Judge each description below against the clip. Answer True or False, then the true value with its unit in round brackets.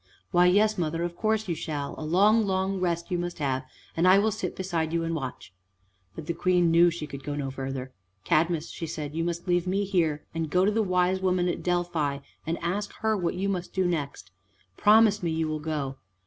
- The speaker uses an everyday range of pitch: True (3.2 semitones)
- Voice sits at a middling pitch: True (175 Hz)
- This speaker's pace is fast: True (220 wpm)